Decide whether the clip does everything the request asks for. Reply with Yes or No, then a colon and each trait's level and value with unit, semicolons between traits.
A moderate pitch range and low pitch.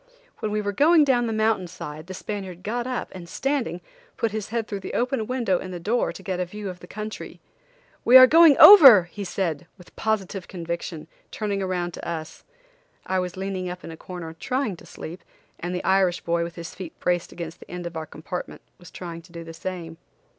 No: average, 3.9 semitones; medium, 185 Hz